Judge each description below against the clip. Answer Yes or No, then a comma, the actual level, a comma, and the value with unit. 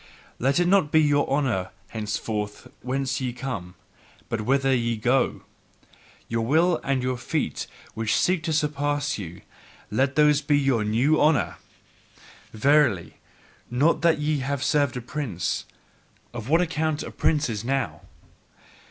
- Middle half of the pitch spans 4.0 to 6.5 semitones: Yes, average, 4.5 semitones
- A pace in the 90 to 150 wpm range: Yes, average, 140 wpm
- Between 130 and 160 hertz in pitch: Yes, low, 135 Hz